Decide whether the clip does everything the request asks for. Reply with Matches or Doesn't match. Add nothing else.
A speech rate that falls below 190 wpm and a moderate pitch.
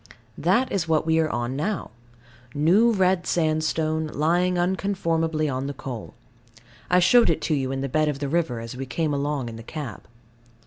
Matches